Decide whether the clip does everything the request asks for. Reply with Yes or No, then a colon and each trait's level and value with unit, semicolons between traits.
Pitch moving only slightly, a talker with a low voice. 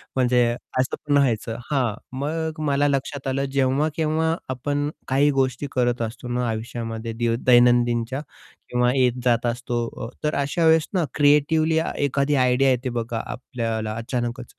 No: average, 3.1 semitones; low, 130 Hz